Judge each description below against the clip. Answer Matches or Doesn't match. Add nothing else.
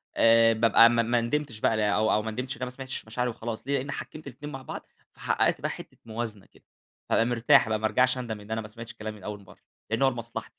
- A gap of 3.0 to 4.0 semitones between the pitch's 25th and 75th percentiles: Doesn't match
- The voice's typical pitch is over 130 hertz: Doesn't match